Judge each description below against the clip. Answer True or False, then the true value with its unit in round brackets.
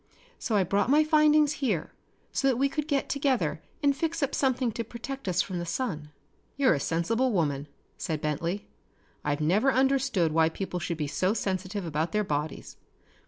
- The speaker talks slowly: False (180 wpm)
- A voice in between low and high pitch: False (210 Hz)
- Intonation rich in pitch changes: True (8.5 semitones)